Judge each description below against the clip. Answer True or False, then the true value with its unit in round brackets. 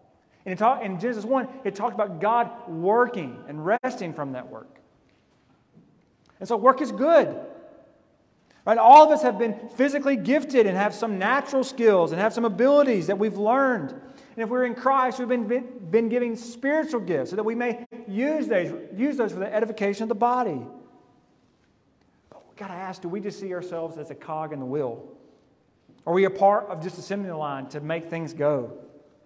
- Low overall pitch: False (225 Hz)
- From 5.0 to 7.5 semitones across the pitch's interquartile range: True (5.3 semitones)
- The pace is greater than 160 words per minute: True (195 wpm)